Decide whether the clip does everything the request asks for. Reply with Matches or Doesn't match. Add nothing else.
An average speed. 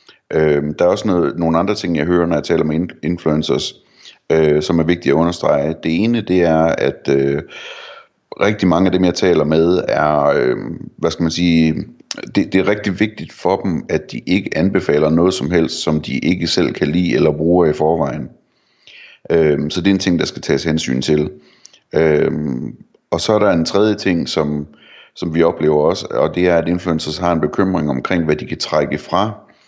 Matches